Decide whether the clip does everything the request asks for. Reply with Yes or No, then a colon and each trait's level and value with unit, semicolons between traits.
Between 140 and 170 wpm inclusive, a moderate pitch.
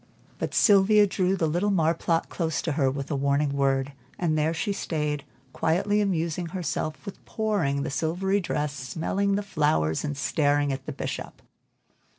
Yes: average, 165 wpm; medium, 160 Hz